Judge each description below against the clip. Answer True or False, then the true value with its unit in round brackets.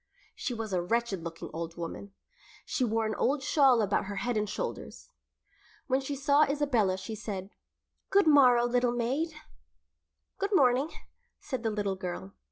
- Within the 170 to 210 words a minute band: False (160 wpm)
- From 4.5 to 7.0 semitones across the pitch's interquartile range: True (5.4 semitones)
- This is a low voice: False (235 Hz)